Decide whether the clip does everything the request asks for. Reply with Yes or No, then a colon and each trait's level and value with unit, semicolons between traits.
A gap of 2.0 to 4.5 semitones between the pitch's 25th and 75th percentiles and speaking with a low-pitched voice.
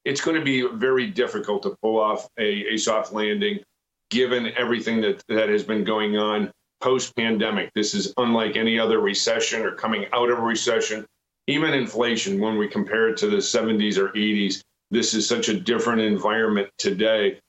Yes: narrow, 2.4 semitones; low, 110 Hz